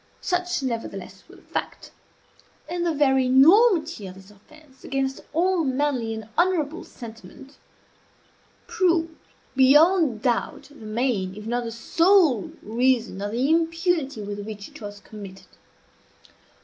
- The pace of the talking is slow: Yes, slow, 130 wpm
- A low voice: No, very high, 265 Hz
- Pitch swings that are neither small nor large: No, wide, 6.8 semitones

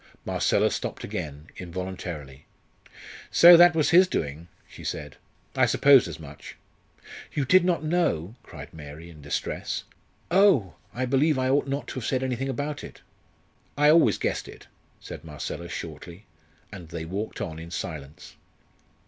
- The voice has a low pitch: Yes, low, 100 Hz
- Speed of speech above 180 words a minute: No, average, 150 wpm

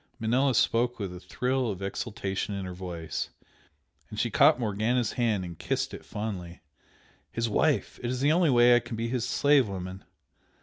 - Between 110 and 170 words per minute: No, average, 180 wpm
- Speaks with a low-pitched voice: Yes, low, 115 Hz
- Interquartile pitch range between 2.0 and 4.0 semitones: No, average, 4.4 semitones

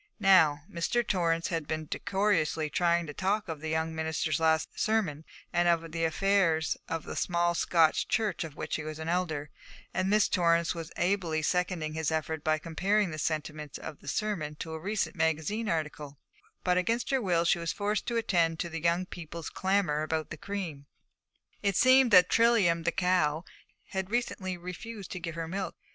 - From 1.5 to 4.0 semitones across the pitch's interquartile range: Yes, average, 3.3 semitones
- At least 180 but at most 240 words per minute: Yes, average, 185 wpm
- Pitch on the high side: No, medium, 170 Hz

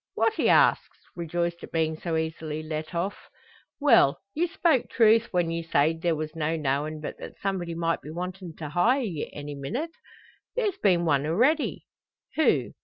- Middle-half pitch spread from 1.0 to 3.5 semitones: No, wide, 5.4 semitones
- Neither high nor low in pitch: Yes, medium, 170 Hz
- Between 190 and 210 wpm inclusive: No, average, 175 wpm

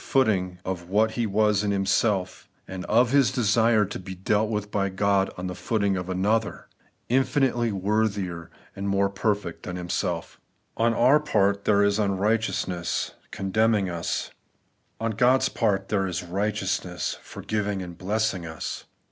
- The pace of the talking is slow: No, average, 145 wpm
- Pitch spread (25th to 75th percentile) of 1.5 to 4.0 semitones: Yes, average, 2.8 semitones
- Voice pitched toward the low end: Yes, low, 100 Hz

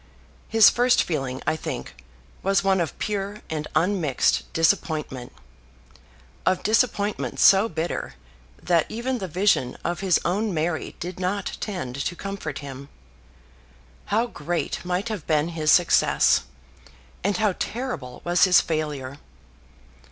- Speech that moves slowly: Yes, slow, 130 wpm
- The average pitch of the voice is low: No, medium, 175 Hz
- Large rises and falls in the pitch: No, average, 4.7 semitones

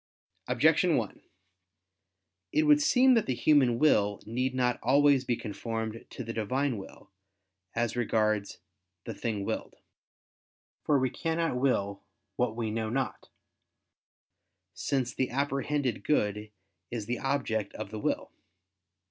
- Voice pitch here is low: Yes, low, 120 Hz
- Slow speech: Yes, slow, 130 wpm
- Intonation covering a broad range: No, average, 4.1 semitones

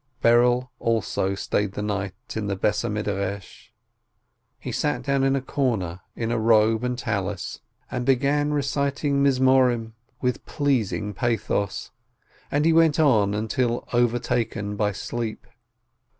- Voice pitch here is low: Yes, low, 115 Hz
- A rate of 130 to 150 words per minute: Yes, slow, 135 wpm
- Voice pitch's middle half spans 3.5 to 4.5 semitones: Yes, average, 4.2 semitones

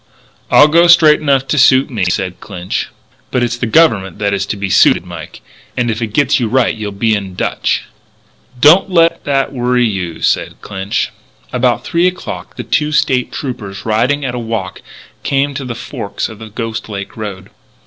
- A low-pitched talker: Yes, low, 120 Hz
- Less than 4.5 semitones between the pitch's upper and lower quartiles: No, average, 5.3 semitones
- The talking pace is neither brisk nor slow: Yes, average, 190 wpm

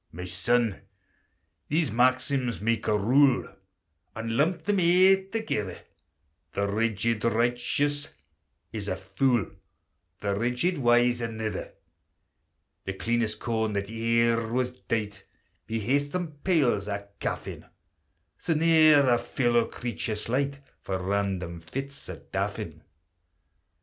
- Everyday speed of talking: No, slow, 120 wpm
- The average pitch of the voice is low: Yes, low, 115 Hz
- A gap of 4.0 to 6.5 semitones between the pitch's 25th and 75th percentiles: Yes, average, 4.7 semitones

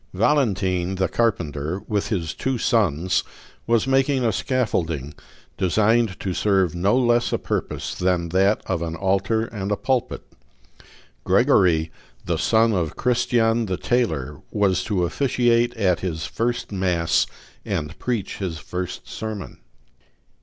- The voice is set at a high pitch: No, low, 100 Hz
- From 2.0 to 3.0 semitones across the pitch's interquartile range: No, average, 4.9 semitones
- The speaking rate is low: Yes, slow, 130 wpm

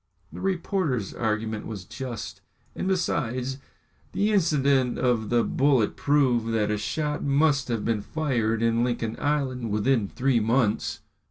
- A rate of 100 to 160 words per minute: Yes, average, 140 wpm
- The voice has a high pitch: No, low, 125 Hz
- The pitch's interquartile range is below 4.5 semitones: Yes, average, 4.1 semitones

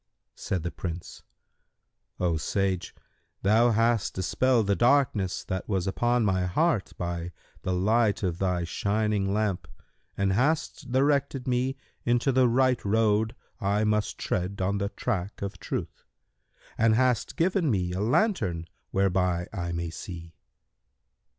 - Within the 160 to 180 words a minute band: No, slow, 135 wpm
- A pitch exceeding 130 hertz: No, low, 100 Hz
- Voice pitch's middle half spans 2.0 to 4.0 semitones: No, average, 4.6 semitones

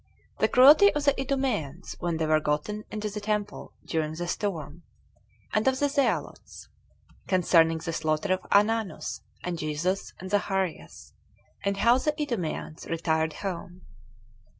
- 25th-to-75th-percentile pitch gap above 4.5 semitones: Yes, average, 5.2 semitones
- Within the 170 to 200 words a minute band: No, average, 140 wpm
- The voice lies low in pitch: No, high, 190 Hz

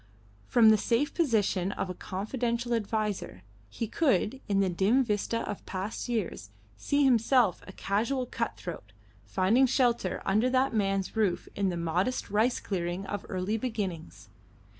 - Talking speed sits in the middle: Yes, average, 150 wpm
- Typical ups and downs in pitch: Yes, average, 4.1 semitones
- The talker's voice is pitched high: Yes, high, 210 Hz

